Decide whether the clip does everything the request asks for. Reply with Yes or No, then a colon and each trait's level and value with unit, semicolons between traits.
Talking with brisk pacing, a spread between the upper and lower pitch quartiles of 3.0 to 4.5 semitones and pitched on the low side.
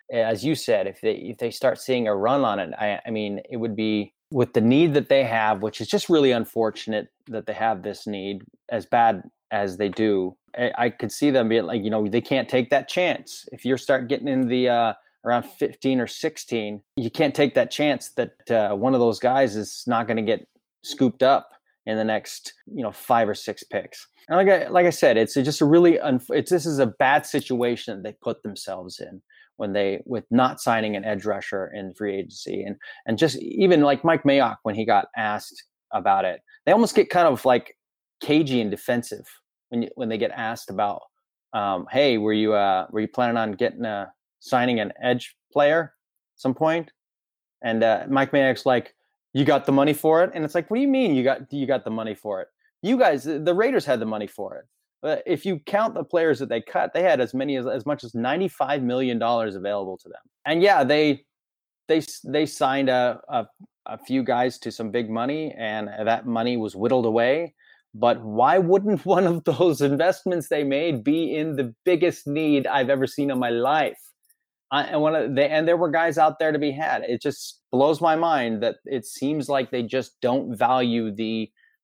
No: fast, 220 wpm; wide, 5.5 semitones; low, 130 Hz